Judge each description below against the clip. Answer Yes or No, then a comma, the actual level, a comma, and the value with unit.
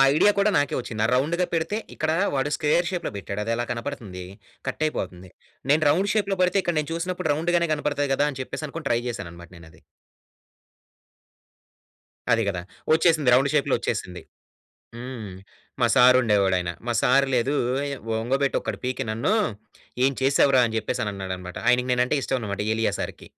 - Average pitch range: No, wide, 5.9 semitones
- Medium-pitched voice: No, low, 130 Hz